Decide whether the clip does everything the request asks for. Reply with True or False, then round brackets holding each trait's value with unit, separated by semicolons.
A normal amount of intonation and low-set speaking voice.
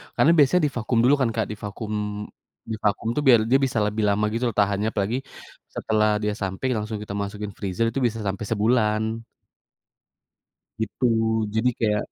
False (2.1 semitones; 110 Hz)